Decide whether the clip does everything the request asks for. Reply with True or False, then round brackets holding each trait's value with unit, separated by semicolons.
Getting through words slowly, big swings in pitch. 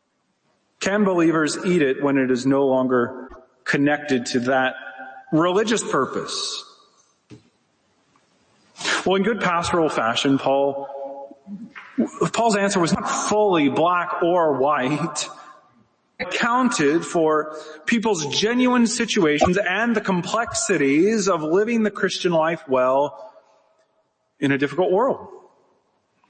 True (110 wpm; 7.3 semitones)